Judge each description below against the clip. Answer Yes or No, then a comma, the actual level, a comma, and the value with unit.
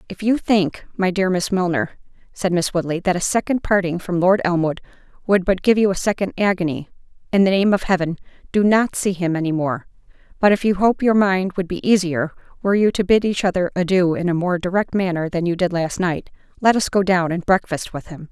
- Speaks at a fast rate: Yes, fast, 225 wpm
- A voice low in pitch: No, medium, 185 Hz